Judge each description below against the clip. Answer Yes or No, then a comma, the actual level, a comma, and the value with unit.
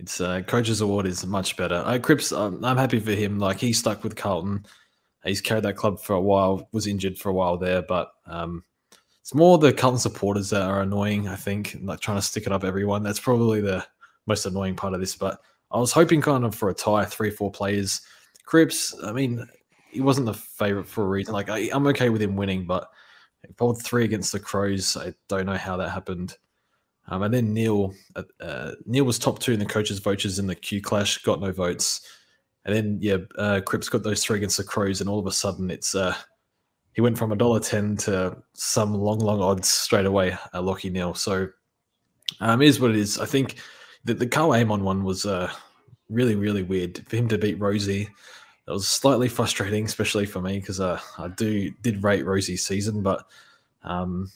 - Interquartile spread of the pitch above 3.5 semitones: No, average, 2.8 semitones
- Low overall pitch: Yes, low, 100 Hz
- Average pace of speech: No, fast, 215 wpm